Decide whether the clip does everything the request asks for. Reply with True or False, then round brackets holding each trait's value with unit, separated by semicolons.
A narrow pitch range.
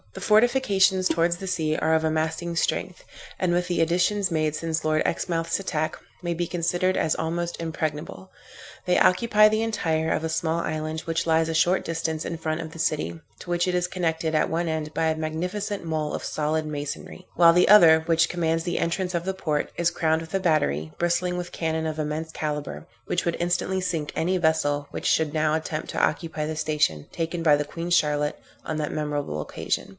True (2.0 semitones)